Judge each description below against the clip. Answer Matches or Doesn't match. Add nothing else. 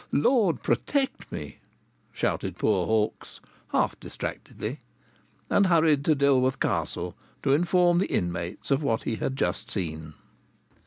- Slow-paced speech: Matches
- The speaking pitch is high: Doesn't match